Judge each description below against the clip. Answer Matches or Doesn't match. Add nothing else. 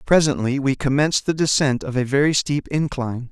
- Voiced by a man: Matches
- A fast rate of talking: Doesn't match